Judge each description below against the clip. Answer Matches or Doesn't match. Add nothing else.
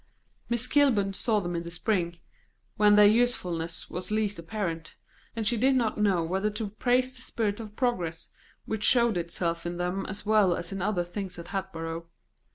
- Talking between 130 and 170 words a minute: Doesn't match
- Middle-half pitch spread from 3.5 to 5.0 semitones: Matches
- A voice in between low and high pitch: Doesn't match